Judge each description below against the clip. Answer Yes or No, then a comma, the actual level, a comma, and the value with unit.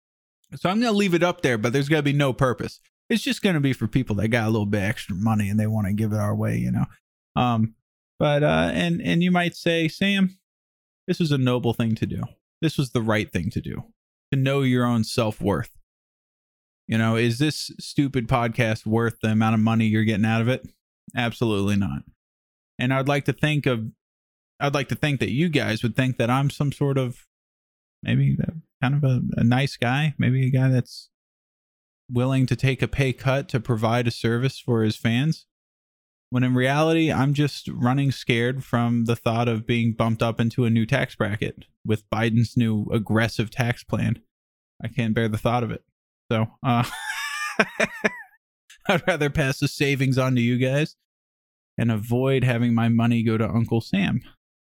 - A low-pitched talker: Yes, low, 120 Hz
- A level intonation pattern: No, average, 3.9 semitones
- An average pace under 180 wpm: No, average, 200 wpm